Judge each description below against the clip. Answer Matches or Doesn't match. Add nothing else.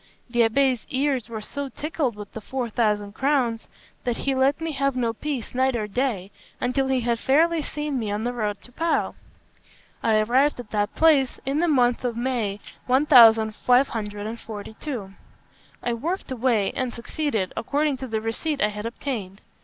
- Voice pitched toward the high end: Matches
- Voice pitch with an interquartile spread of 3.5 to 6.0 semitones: Matches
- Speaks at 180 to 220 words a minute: Doesn't match